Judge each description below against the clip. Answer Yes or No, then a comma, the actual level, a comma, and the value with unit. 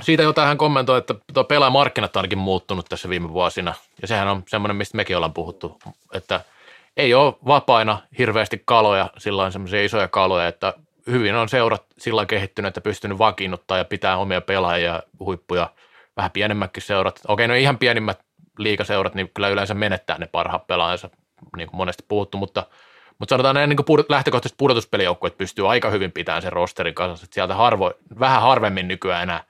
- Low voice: Yes, low, 100 Hz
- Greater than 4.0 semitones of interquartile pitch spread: Yes, average, 4.6 semitones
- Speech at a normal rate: No, fast, 175 wpm